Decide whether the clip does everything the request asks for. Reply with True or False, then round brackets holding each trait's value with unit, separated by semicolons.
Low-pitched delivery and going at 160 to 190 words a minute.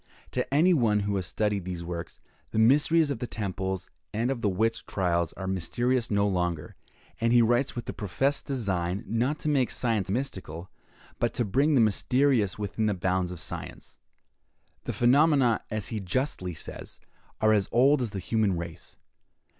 True (110 Hz; 175 wpm)